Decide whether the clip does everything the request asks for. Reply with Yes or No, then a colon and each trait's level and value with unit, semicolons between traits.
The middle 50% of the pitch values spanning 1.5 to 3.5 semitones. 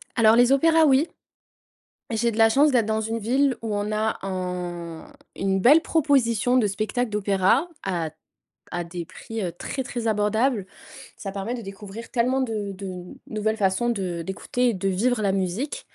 No: average, 4.2 semitones